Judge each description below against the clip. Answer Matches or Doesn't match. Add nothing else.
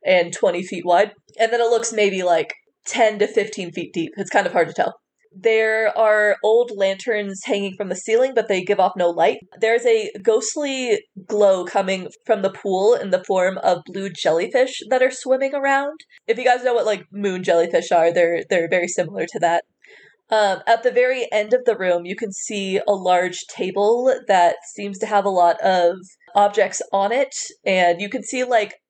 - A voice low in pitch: Doesn't match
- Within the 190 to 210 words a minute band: Matches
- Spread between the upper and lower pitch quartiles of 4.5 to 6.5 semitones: Doesn't match